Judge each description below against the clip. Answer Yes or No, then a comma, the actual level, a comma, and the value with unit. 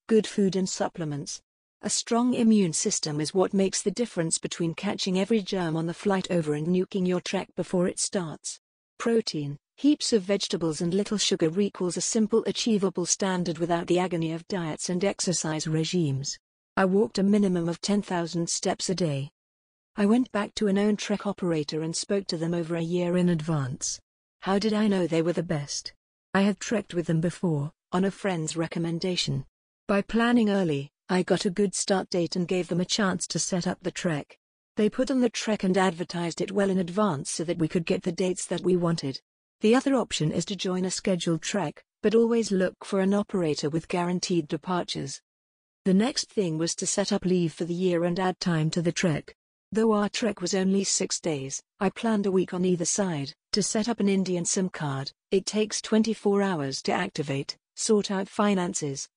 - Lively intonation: No, average, 3.2 semitones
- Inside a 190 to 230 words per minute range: Yes, average, 200 wpm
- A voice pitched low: No, medium, 185 Hz